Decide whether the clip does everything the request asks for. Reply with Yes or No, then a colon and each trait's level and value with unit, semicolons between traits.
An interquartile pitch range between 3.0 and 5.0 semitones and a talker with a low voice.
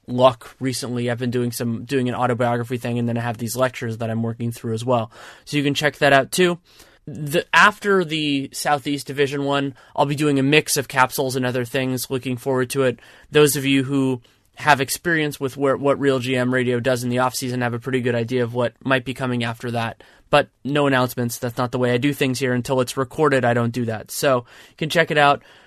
No: narrow, 2.6 semitones; low, 130 Hz